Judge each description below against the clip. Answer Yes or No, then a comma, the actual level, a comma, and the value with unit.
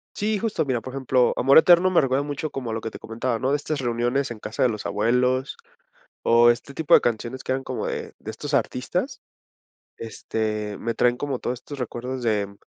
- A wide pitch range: No, average, 3.2 semitones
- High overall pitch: No, low, 125 Hz